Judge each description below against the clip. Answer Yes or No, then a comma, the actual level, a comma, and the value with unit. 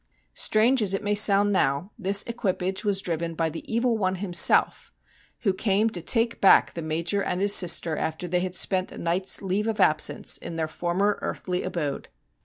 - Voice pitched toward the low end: No, high, 190 Hz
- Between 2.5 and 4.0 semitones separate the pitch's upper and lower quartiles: Yes, average, 3.1 semitones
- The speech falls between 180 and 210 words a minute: Yes, average, 190 wpm